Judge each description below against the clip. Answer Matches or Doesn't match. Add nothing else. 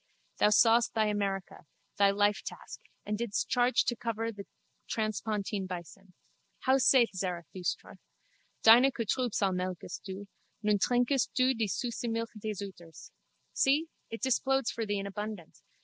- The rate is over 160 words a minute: Doesn't match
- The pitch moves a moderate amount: Matches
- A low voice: Doesn't match